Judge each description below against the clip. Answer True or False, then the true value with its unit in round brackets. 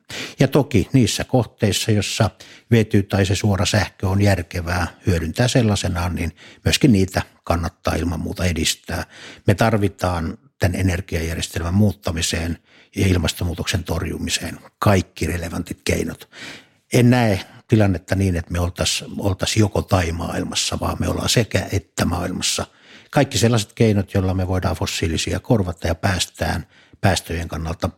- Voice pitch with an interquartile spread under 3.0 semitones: False (3.4 semitones)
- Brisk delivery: False (130 wpm)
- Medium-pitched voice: False (95 Hz)